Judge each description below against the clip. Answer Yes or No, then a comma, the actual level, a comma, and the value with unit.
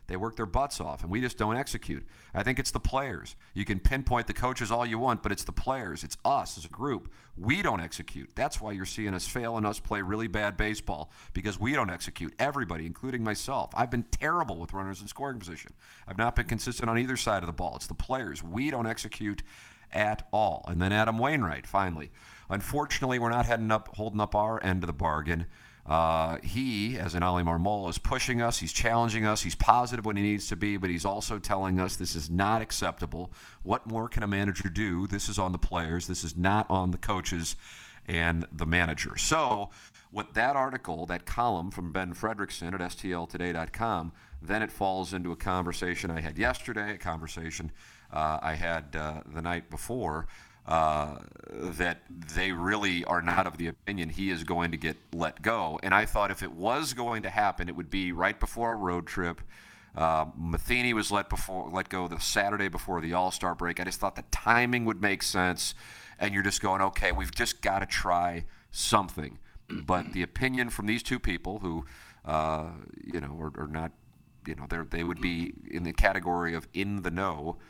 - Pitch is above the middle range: No, very low, 95 Hz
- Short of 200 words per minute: No, fast, 205 wpm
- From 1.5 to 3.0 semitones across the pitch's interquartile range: No, average, 4.2 semitones